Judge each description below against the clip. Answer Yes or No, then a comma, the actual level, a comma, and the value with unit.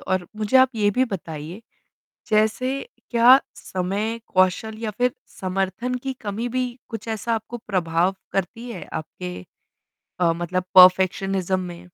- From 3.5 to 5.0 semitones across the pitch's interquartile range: Yes, average, 4.1 semitones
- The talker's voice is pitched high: Yes, high, 200 Hz